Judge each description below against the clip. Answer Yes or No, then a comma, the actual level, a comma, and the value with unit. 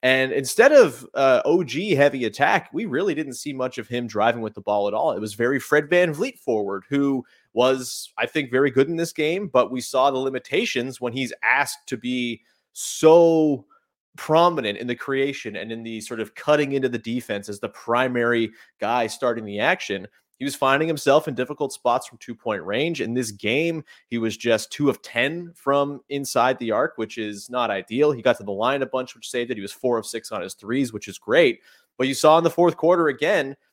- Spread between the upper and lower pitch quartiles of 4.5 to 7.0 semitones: No, average, 3.8 semitones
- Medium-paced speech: No, fast, 220 wpm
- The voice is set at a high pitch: No, low, 130 Hz